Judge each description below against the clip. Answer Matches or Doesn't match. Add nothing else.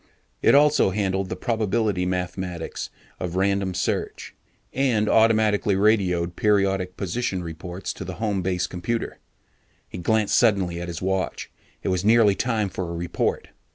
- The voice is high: Doesn't match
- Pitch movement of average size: Matches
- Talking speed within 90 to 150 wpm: Matches